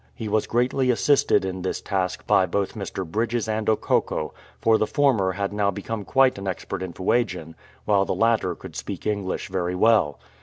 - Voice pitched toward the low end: Yes, low, 100 Hz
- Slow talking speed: No, average, 185 wpm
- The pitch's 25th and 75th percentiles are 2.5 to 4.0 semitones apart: Yes, average, 3.3 semitones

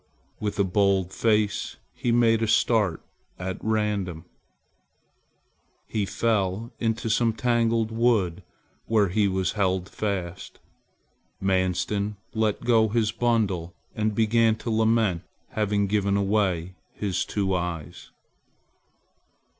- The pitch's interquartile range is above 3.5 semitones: No, average, 2.9 semitones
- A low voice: Yes, low, 105 Hz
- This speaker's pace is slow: Yes, slow, 110 wpm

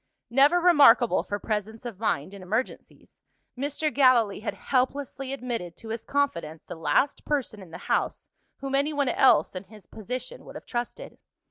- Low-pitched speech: No, high, 245 Hz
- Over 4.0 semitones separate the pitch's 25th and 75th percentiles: Yes, average, 5.2 semitones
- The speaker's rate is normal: Yes, average, 160 wpm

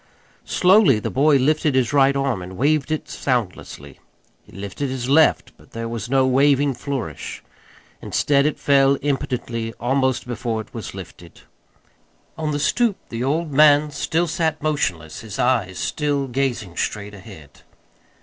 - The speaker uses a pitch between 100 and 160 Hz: Yes, low, 135 Hz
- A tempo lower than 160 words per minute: Yes, average, 150 wpm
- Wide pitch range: No, average, 4.2 semitones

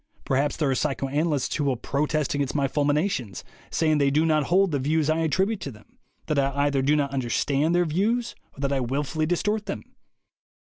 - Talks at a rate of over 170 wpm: Yes, fast, 205 wpm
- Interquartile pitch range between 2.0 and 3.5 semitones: Yes, average, 2.8 semitones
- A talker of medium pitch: Yes, medium, 150 Hz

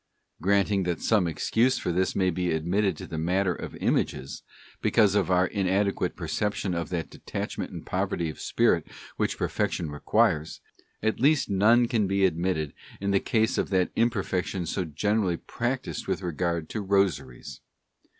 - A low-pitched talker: Yes, very low, 95 Hz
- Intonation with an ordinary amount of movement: Yes, average, 3.4 semitones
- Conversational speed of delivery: Yes, average, 160 wpm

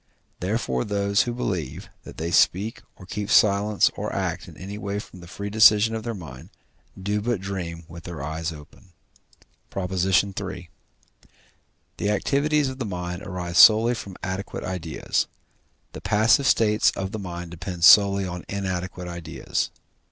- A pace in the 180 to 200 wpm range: No, average, 155 wpm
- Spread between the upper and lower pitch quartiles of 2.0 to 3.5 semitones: Yes, average, 3.0 semitones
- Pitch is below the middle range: Yes, very low, 95 Hz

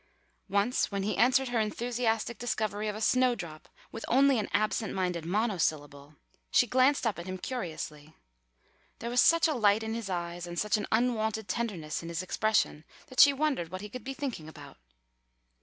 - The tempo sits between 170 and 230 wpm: Yes, average, 180 wpm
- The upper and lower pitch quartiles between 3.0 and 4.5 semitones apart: No, average, 5.3 semitones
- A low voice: No, high, 215 Hz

